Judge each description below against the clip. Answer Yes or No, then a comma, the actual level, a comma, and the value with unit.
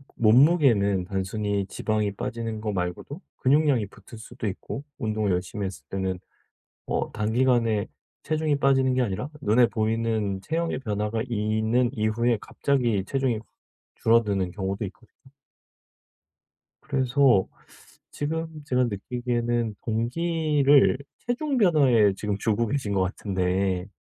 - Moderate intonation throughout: Yes, average, 4.4 semitones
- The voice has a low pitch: Yes, low, 115 Hz